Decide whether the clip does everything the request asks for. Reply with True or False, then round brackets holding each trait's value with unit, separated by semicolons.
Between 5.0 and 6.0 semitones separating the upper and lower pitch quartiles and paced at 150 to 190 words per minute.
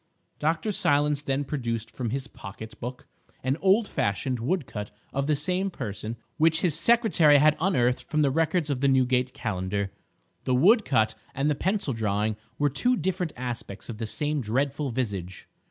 True (5.3 semitones; 165 wpm)